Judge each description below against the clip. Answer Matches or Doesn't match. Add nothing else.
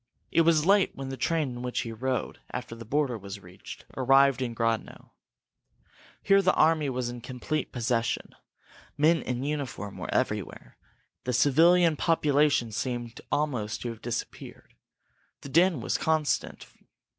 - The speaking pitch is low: Matches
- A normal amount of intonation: Matches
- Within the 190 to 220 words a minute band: Doesn't match